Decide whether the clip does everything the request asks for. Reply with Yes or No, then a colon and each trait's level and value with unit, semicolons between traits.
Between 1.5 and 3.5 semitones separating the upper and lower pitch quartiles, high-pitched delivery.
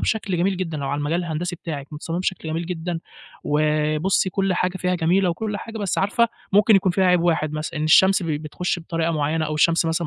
No: average, 3.2 semitones; medium, 170 Hz